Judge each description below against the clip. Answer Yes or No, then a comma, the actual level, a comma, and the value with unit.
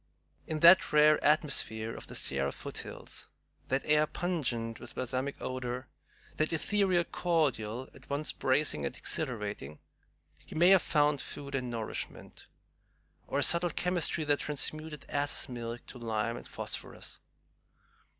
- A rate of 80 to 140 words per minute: Yes, slow, 135 wpm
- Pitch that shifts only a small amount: No, average, 4.5 semitones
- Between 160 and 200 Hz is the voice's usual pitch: No, medium, 140 Hz